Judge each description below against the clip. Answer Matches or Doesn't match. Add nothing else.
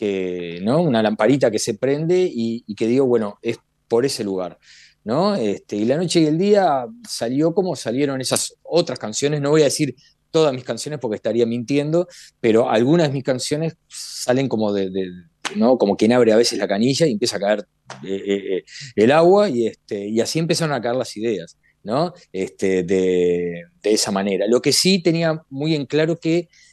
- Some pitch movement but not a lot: Doesn't match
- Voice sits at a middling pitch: Doesn't match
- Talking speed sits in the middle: Doesn't match